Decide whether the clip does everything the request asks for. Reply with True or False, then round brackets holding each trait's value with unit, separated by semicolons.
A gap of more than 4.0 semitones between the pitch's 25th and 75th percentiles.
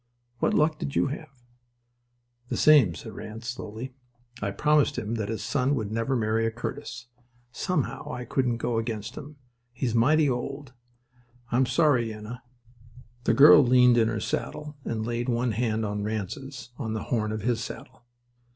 False (3.5 semitones)